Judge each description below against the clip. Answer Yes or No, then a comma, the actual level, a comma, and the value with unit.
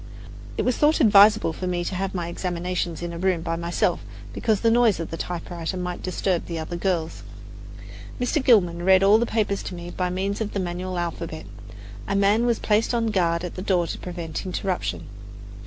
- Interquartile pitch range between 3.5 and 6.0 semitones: No, average, 2.8 semitones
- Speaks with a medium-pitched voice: Yes, medium, 180 Hz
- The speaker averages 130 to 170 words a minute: No, average, 200 wpm